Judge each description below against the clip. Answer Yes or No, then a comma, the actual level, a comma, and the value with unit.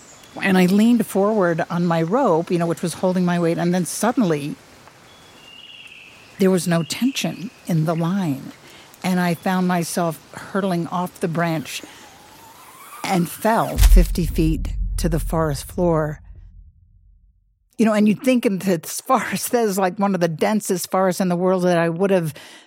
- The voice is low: No, medium, 180 Hz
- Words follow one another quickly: No, average, 165 wpm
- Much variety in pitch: No, average, 3.0 semitones